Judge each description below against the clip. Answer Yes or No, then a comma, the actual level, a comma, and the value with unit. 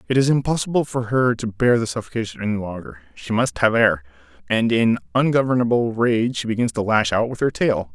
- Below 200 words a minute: No, fast, 205 wpm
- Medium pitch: No, low, 115 Hz